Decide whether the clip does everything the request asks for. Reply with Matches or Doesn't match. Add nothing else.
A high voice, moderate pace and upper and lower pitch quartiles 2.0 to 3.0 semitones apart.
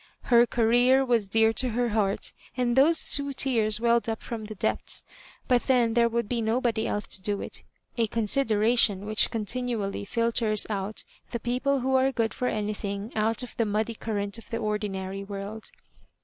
Matches